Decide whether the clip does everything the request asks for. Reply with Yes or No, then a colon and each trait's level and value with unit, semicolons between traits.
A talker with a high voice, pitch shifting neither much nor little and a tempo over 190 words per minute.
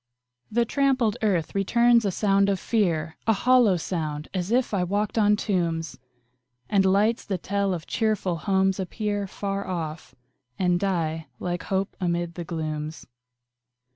No: high, 195 Hz; average, 3.4 semitones; average, 145 wpm